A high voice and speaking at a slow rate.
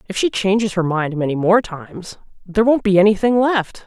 No: high, 195 Hz; average, 200 wpm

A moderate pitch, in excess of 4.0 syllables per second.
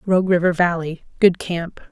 Yes: medium, 175 Hz; 5.0 syllables/s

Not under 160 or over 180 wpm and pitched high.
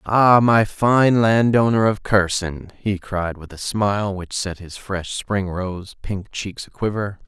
No: average, 175 wpm; low, 100 Hz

